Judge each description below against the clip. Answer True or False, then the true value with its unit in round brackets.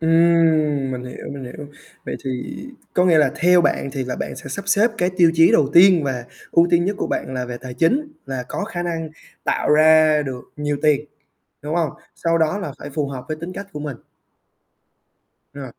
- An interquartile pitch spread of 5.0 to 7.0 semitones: False (4.1 semitones)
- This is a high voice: False (155 Hz)